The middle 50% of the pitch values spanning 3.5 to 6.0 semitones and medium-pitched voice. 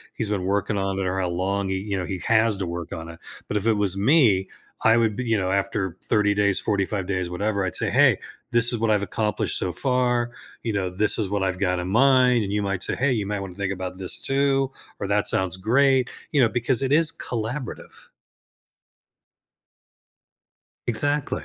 No: average, 3.8 semitones; low, 105 Hz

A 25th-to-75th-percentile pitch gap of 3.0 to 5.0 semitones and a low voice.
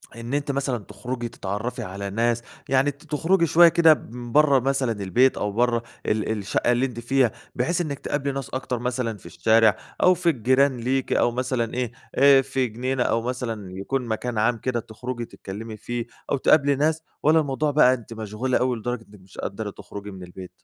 Yes: average, 3.5 semitones; low, 125 Hz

